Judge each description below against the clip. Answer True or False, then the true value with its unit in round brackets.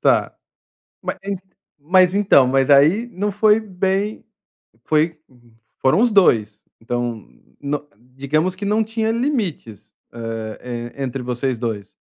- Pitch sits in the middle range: True (150 Hz)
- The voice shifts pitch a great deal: True (8.7 semitones)